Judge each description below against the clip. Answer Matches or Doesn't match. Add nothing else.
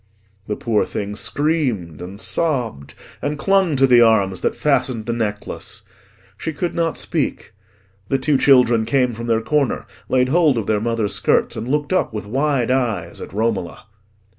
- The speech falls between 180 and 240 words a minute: Doesn't match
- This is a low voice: Matches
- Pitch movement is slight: Doesn't match